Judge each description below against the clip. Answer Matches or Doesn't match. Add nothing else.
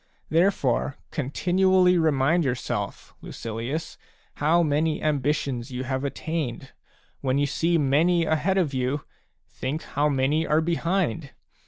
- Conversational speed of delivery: Doesn't match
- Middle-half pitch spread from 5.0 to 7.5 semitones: Doesn't match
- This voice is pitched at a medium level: Matches